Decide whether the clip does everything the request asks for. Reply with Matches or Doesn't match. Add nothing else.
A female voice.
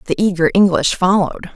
Matches